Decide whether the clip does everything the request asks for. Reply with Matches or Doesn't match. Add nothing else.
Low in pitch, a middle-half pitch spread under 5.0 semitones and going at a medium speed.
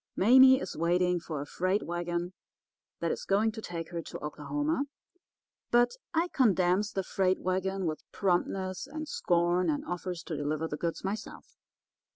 Doesn't match